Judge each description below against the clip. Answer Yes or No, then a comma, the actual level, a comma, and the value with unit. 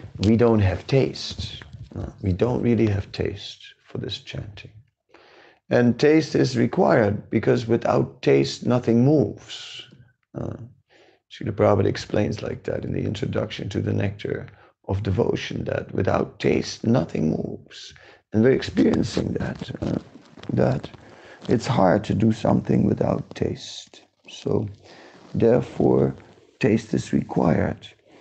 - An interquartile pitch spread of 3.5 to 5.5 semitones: No, average, 3.0 semitones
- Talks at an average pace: No, slow, 130 wpm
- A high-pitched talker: No, low, 110 Hz